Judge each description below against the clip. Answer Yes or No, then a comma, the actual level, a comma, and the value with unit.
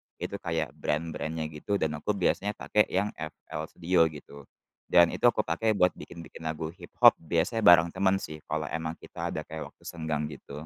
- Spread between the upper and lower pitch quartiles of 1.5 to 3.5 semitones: Yes, average, 3.0 semitones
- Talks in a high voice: No, very low, 85 Hz